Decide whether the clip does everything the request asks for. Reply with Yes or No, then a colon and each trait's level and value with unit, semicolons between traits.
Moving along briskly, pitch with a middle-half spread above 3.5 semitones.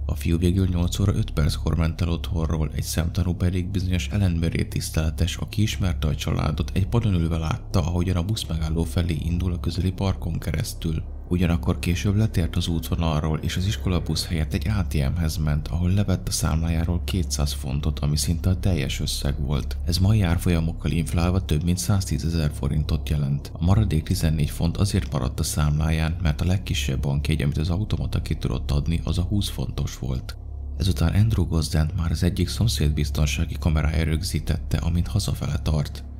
No: fast, 170 wpm; average, 2.8 semitones